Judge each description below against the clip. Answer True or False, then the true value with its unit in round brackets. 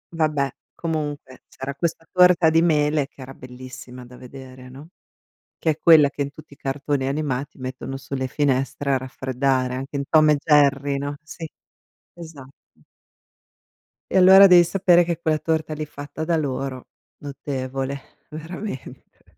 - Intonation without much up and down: False (3.1 semitones)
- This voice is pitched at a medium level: True (145 Hz)